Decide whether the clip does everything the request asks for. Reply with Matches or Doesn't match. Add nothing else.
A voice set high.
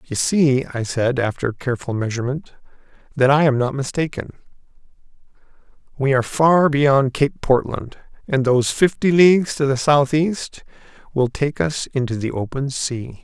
Doesn't match